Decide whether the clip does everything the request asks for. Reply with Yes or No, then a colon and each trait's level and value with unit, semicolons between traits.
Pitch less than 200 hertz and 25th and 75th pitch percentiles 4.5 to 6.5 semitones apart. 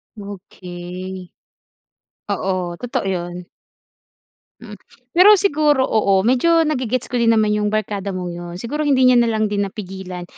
No: high, 210 Hz; average, 5.2 semitones